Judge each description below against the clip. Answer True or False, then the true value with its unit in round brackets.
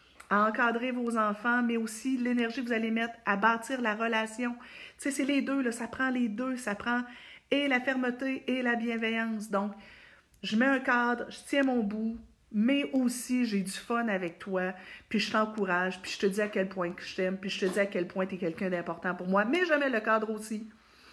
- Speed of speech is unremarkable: False (225 wpm)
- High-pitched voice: True (225 Hz)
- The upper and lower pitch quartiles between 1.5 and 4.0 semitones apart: True (3.6 semitones)